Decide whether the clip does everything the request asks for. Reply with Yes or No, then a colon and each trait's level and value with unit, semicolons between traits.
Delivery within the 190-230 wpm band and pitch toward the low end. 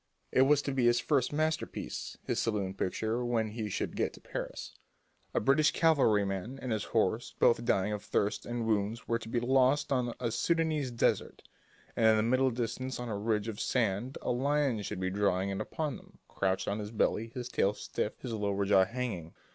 Yes: average, 200 wpm; low, 115 Hz